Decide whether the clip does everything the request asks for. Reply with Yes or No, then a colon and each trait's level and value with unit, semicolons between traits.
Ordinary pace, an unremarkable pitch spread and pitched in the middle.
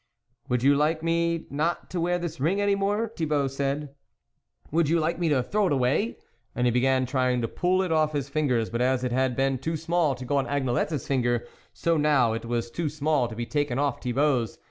No: fast, 235 wpm; average, 4.6 semitones; medium, 145 Hz